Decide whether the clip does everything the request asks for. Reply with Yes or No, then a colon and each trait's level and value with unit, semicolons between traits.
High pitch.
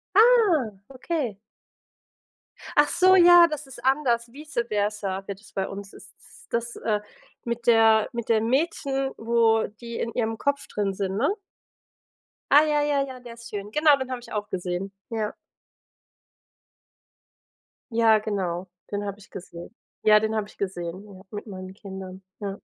Yes: high, 225 Hz